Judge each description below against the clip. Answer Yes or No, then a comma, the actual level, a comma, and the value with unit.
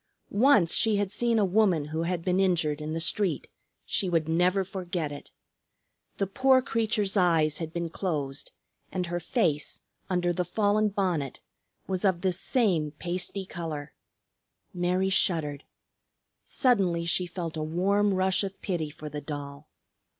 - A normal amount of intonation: Yes, average, 3.6 semitones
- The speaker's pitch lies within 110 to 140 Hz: No, medium, 180 Hz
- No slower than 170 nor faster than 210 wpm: No, average, 150 wpm